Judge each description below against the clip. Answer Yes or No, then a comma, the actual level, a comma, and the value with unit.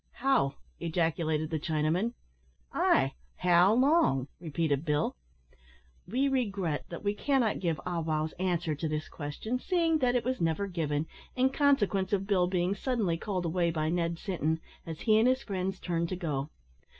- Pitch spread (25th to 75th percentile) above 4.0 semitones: Yes, average, 5.3 semitones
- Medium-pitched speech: Yes, medium, 180 Hz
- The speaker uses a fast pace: No, average, 160 wpm